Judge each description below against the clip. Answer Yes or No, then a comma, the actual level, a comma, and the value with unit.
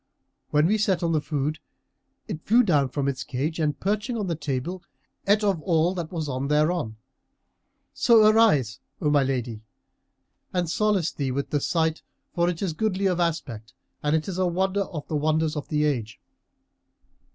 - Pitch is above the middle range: No, medium, 160 Hz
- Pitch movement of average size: Yes, average, 4.4 semitones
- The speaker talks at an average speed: Yes, average, 175 wpm